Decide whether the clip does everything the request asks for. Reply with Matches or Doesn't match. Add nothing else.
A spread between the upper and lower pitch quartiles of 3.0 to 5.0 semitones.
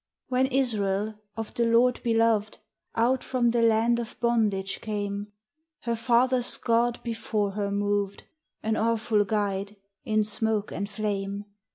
Doesn't match